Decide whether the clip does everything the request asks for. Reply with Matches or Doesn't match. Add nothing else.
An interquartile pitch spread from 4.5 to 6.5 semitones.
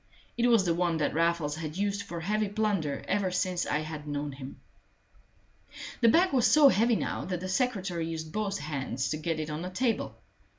Matches